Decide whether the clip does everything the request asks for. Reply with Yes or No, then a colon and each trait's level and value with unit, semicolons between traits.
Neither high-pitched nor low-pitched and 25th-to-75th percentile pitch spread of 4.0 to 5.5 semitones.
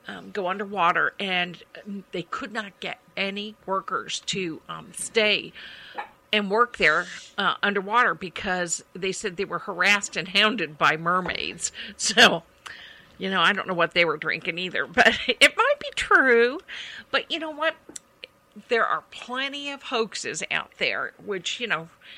No: high, 205 Hz; average, 4.9 semitones